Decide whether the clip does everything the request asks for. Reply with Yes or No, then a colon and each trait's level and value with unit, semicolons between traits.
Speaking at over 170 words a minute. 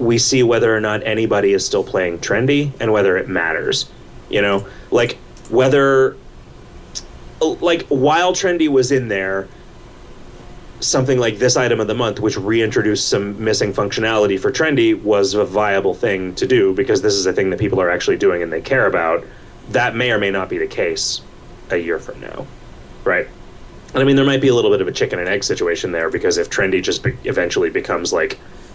Yes: average, 200 wpm